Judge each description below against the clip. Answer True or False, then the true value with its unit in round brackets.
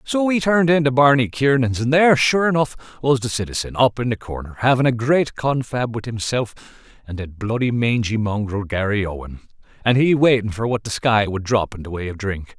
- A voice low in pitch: True (120 Hz)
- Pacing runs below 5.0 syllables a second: False (5.5 syllables/s)